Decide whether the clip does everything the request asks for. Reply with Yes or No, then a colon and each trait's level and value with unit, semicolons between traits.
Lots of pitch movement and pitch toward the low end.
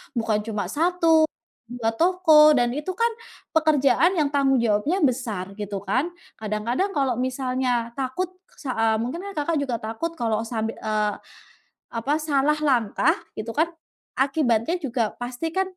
No: wide, 5.7 semitones; very high, 260 Hz